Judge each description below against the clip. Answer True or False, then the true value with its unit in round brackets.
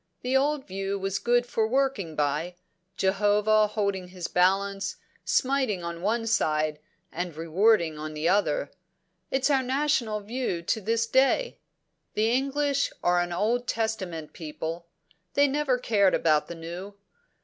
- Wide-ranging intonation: True (6.0 semitones)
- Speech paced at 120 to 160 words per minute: True (140 wpm)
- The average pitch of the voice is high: True (200 Hz)